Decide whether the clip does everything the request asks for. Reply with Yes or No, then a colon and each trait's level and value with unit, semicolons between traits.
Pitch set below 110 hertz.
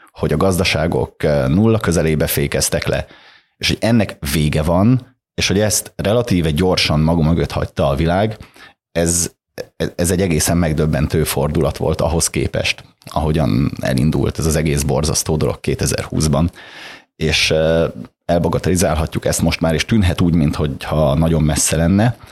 Yes: very low, 85 Hz